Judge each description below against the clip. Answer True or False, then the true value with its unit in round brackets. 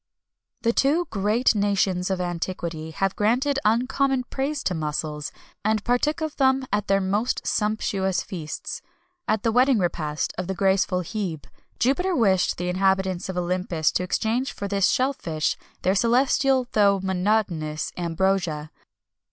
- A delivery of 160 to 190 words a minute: False (145 wpm)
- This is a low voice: False (195 Hz)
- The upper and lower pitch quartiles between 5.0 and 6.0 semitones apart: True (5.3 semitones)